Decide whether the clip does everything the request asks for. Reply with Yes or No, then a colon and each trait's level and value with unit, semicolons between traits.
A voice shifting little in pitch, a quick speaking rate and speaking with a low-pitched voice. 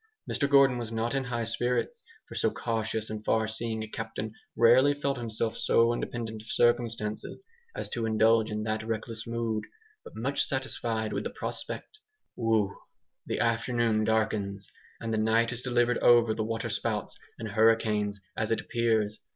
No: narrow, 1.4 semitones; average, 165 wpm; low, 115 Hz